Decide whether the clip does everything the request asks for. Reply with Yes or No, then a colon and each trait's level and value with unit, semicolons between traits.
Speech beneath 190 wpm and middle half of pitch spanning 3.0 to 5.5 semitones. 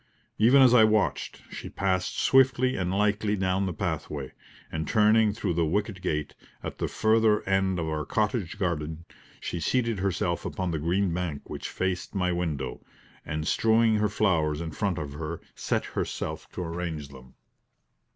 Yes: average, 165 wpm; average, 4.5 semitones